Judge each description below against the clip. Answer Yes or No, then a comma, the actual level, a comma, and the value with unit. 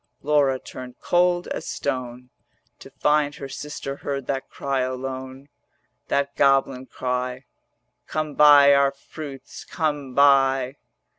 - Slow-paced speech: Yes, slow, 120 wpm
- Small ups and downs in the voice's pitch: Yes, narrow, 1.7 semitones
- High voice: No, low, 135 Hz